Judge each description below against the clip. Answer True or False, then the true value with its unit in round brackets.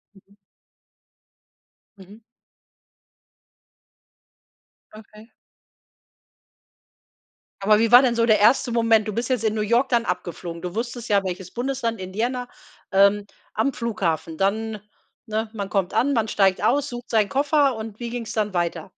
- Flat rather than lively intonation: False (3.2 semitones)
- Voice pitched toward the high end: True (220 Hz)